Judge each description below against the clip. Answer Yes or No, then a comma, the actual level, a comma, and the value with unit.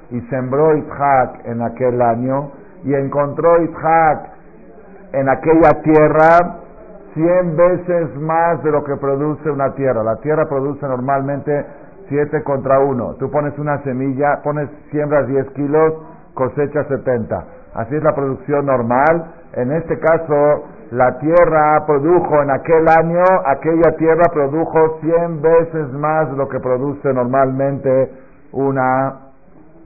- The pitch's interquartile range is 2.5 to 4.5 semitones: Yes, average, 2.9 semitones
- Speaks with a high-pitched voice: No, medium, 145 Hz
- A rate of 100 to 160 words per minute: Yes, average, 130 wpm